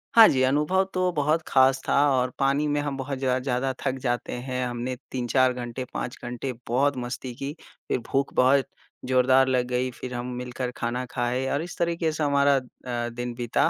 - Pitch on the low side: Yes, low, 130 Hz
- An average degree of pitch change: No, narrow, 2.1 semitones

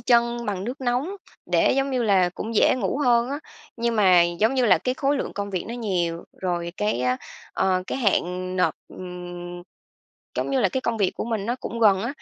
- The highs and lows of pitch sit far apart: No, average, 5.0 semitones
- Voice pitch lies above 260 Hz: No, high, 210 Hz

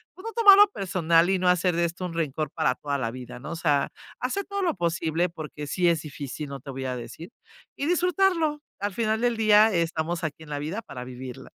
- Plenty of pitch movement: Yes, wide, 6.6 semitones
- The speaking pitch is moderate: Yes, medium, 170 Hz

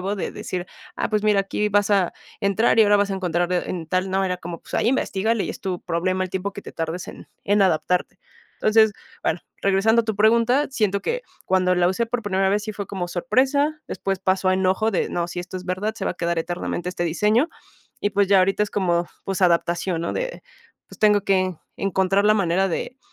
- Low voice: No, high, 195 Hz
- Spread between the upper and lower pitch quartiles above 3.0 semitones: No, narrow, 2.6 semitones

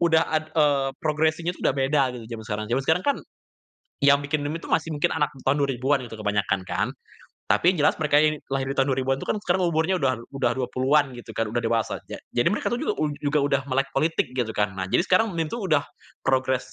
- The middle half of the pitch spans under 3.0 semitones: No, average, 3.4 semitones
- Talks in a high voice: No, medium, 140 Hz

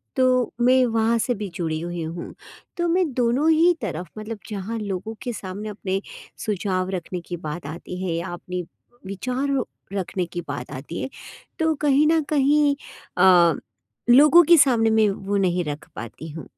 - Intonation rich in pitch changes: Yes, wide, 6.6 semitones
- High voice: Yes, high, 205 Hz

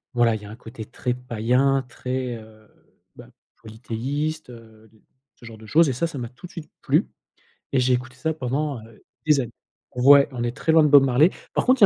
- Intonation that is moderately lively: Yes, average, 3.8 semitones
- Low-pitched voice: Yes, low, 125 Hz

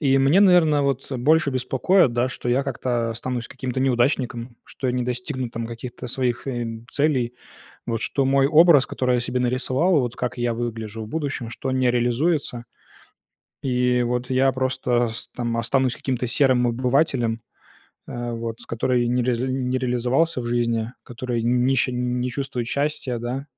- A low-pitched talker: Yes, low, 125 Hz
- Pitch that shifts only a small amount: Yes, narrow, 1.9 semitones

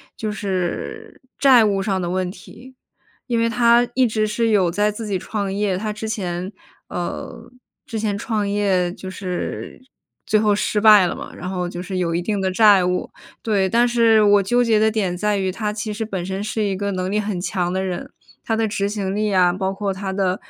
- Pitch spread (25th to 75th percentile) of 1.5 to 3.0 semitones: Yes, narrow, 2.6 semitones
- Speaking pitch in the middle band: No, high, 205 Hz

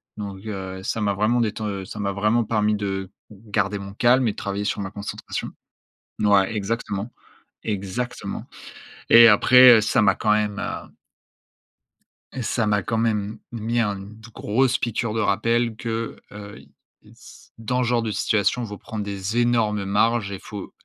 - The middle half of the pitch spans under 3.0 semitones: Yes, narrow, 2.4 semitones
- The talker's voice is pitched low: Yes, low, 105 Hz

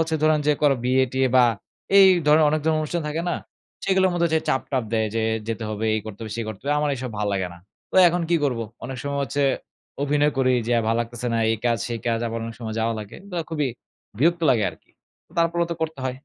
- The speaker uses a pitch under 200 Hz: Yes, low, 135 Hz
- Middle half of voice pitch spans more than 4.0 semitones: Yes, wide, 5.4 semitones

